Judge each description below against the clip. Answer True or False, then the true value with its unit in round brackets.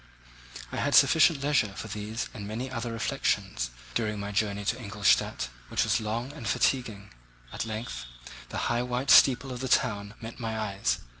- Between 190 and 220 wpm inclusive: False (170 wpm)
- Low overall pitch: True (110 Hz)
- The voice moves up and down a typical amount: True (3.3 semitones)